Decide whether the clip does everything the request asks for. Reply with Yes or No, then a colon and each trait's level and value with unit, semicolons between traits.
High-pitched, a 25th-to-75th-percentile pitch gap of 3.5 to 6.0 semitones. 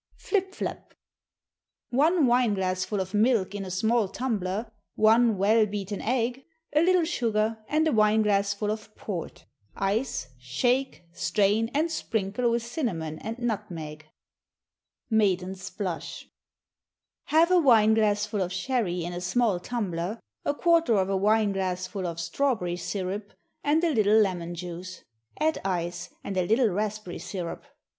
Yes: high, 210 Hz; average, 4.4 semitones